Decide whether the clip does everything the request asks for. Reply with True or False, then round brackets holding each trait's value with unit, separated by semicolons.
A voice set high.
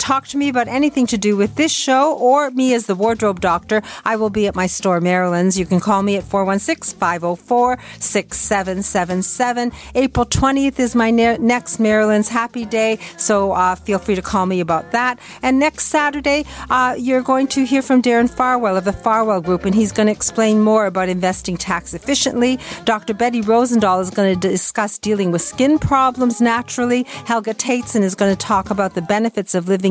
True (220 Hz)